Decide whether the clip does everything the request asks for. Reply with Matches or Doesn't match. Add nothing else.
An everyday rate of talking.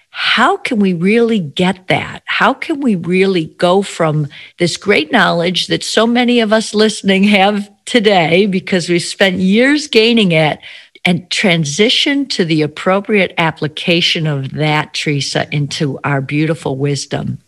Matches